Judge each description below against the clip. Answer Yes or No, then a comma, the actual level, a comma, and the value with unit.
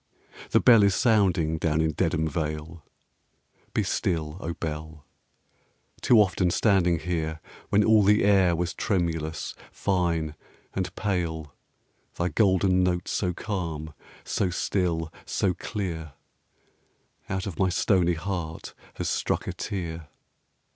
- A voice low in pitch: Yes, very low, 85 Hz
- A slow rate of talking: Yes, slow, 125 wpm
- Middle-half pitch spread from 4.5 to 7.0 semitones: No, average, 3.1 semitones